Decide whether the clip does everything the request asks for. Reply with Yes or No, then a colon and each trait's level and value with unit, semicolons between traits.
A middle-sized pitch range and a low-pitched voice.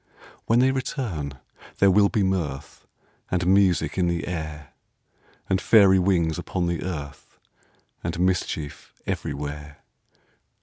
Yes: average, 3.9 semitones; very low, 90 Hz